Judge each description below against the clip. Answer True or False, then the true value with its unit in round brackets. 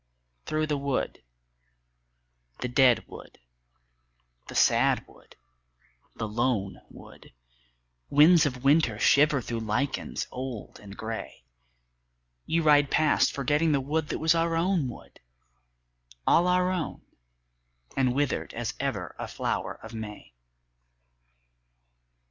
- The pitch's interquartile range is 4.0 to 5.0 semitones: True (4.7 semitones)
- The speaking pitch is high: False (140 Hz)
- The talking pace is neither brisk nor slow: False (115 wpm)